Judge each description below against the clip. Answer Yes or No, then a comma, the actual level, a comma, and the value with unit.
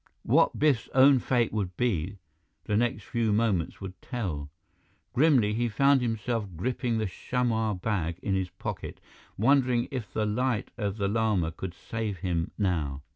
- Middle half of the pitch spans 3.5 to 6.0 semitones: Yes, average, 4.2 semitones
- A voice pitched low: Yes, low, 110 Hz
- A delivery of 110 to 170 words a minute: Yes, average, 155 wpm